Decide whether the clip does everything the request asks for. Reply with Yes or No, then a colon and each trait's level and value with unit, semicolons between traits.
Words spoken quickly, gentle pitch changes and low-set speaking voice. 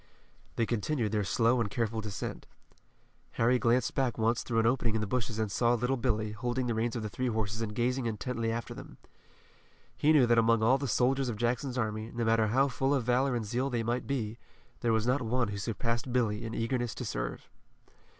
Yes: fast, 215 wpm; narrow, 2.1 semitones; low, 115 Hz